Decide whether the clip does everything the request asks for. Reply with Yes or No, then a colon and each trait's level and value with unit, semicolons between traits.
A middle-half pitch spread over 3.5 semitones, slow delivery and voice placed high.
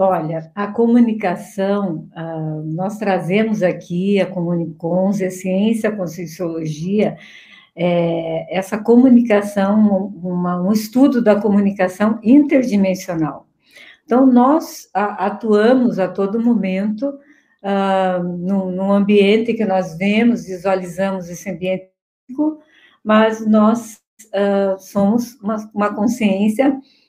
No: average, 3.2 semitones; slow, 100 wpm; high, 200 Hz